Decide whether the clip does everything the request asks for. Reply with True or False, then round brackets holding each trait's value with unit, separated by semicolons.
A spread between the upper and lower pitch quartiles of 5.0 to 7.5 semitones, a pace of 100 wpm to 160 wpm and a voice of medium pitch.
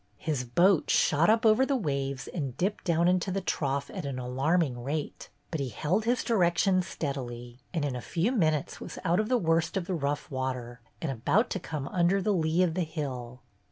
False (5.3 semitones; 205 wpm; 160 Hz)